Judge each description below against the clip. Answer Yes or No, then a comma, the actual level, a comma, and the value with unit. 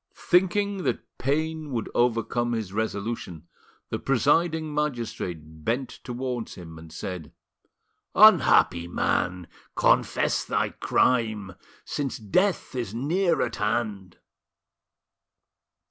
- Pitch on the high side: No, low, 120 Hz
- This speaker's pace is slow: Yes, slow, 100 wpm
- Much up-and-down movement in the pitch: Yes, wide, 7.4 semitones